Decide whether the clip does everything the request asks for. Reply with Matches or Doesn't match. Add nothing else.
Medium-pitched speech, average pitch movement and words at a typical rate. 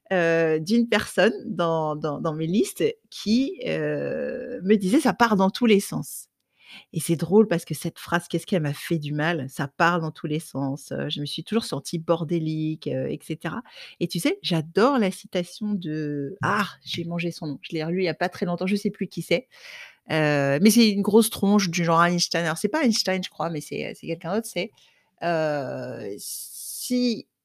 Matches